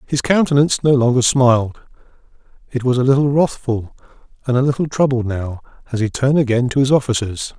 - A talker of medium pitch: No, low, 130 Hz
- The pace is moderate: Yes, average, 175 wpm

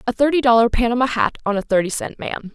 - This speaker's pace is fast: Yes, fast, 235 wpm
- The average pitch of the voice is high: Yes, high, 235 Hz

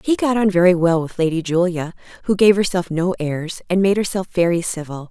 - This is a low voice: No, medium, 180 Hz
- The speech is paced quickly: Yes, fast, 210 wpm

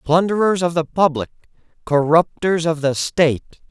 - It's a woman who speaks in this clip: No, male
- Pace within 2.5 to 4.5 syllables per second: No, 5.0 syllables/s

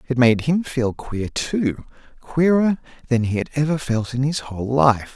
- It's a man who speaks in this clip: Yes, male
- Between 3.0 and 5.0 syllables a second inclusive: Yes, 4.5 syllables/s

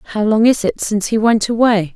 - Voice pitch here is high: Yes, high, 215 Hz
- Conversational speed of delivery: No, fast, 245 wpm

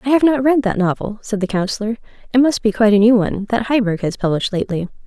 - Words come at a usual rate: No, fast, 250 wpm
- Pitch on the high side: Yes, high, 220 Hz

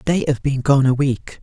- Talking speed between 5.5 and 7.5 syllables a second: No, 4.8 syllables/s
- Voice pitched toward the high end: No, low, 135 Hz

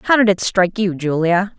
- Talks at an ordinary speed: No, fast, 230 wpm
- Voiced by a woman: Yes, female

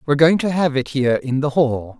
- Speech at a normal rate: No, fast, 270 wpm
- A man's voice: Yes, male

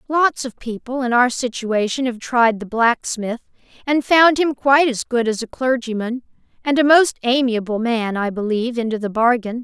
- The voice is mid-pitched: No, high, 240 Hz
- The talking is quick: No, average, 180 wpm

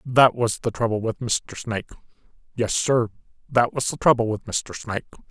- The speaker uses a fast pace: No, average, 180 wpm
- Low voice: Yes, low, 115 Hz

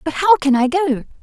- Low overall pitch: No, very high, 305 Hz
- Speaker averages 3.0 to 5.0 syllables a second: No, 5.2 syllables/s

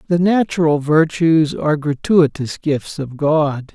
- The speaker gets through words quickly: No, slow, 130 wpm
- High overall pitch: No, medium, 155 Hz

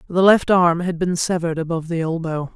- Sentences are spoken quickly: Yes, fast, 210 wpm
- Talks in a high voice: No, medium, 170 Hz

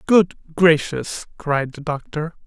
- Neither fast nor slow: No, slow, 120 wpm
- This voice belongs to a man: Yes, male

